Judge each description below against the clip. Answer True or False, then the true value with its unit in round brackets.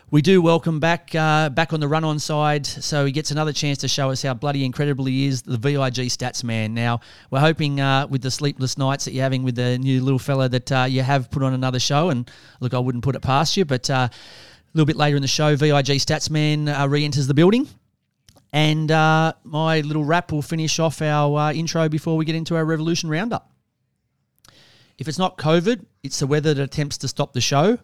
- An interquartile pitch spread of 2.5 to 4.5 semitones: True (2.9 semitones)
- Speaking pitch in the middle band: True (145 Hz)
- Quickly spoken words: True (235 wpm)